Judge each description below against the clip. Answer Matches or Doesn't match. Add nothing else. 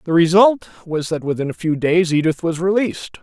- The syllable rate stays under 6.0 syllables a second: Matches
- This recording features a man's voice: Matches